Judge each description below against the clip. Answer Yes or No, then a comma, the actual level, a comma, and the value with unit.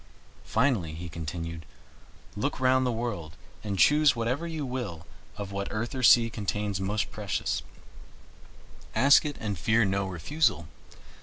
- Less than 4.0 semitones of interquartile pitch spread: No, average, 5.2 semitones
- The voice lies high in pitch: No, low, 110 Hz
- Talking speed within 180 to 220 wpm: No, average, 140 wpm